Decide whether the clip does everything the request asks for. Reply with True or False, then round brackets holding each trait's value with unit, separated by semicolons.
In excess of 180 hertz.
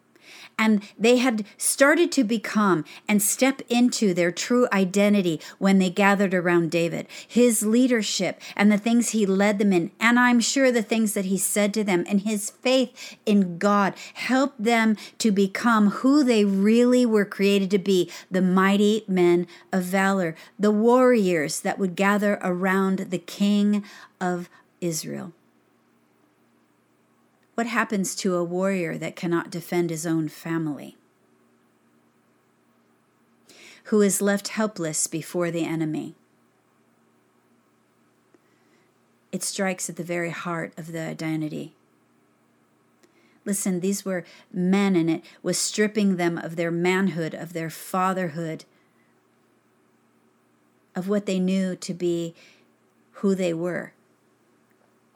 True (190 Hz)